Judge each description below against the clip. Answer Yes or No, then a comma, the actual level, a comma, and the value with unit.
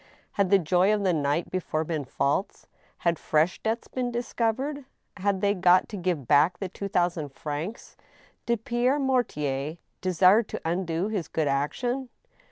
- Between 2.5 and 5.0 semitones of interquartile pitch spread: No, wide, 5.6 semitones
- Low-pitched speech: No, medium, 185 Hz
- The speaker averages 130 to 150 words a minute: No, average, 160 wpm